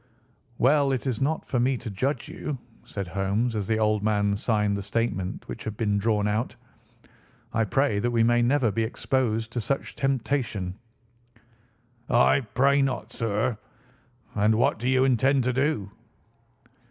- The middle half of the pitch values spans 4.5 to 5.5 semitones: No, average, 4.0 semitones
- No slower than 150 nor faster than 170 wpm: Yes, average, 165 wpm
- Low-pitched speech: Yes, low, 115 Hz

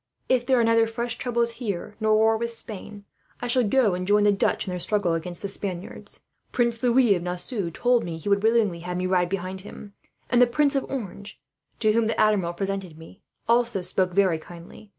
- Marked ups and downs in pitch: No, average, 4.3 semitones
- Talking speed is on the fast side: Yes, fast, 220 wpm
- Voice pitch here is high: Yes, high, 205 Hz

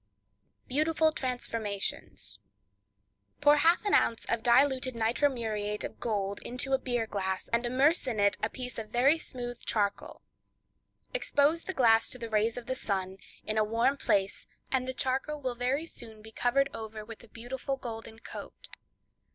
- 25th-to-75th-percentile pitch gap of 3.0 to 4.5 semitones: Yes, average, 3.4 semitones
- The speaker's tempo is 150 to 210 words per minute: Yes, average, 160 wpm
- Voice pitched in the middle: No, high, 240 Hz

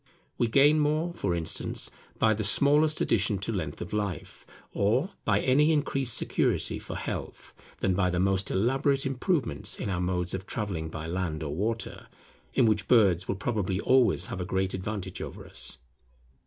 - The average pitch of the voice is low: Yes, low, 100 Hz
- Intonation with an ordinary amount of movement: No, wide, 6.0 semitones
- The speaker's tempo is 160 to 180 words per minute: Yes, average, 170 wpm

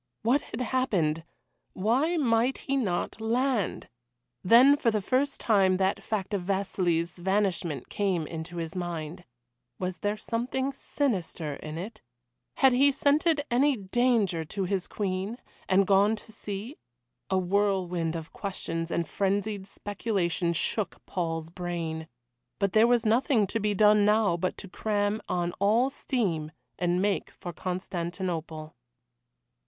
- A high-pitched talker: Yes, high, 195 Hz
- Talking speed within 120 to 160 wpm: Yes, average, 140 wpm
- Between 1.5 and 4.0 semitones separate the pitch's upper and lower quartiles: No, average, 4.6 semitones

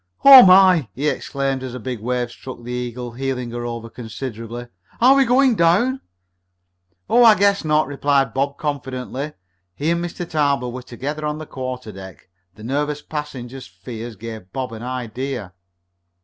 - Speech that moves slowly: No, average, 160 wpm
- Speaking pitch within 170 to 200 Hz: No, low, 130 Hz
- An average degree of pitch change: Yes, average, 4.1 semitones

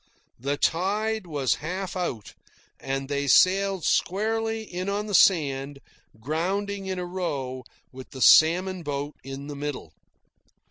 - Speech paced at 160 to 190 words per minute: No, slow, 135 wpm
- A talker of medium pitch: Yes, medium, 170 Hz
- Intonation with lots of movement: Yes, wide, 5.7 semitones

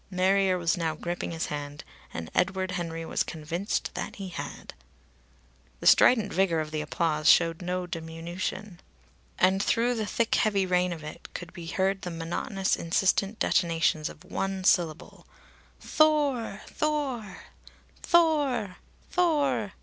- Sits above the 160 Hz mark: Yes, medium, 185 Hz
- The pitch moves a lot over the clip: No, average, 3.8 semitones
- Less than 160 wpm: Yes, average, 140 wpm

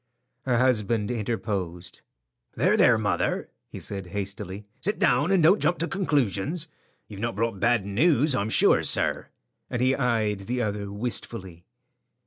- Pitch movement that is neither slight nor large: Yes, average, 4.4 semitones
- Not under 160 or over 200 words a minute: No, average, 145 wpm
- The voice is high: No, low, 115 Hz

